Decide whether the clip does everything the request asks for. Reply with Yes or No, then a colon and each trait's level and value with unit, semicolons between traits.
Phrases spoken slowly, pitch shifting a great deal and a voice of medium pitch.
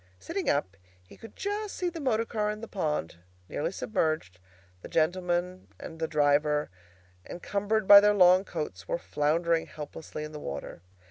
No: average, 160 wpm; wide, 5.8 semitones; medium, 175 Hz